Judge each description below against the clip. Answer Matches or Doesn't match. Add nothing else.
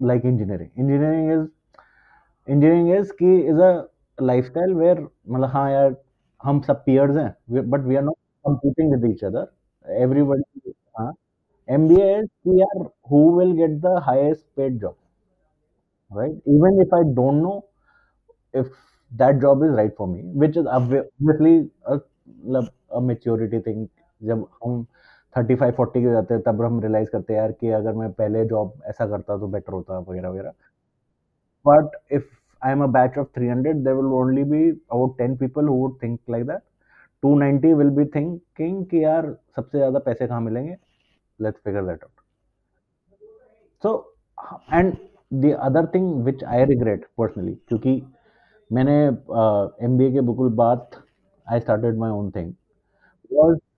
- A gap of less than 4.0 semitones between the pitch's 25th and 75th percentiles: Doesn't match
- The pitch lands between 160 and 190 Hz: Doesn't match